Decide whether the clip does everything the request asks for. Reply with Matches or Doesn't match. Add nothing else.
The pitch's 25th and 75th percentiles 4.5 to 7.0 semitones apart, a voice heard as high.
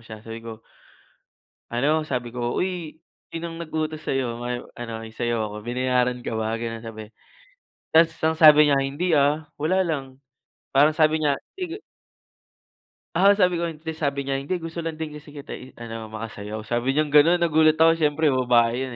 Doesn't match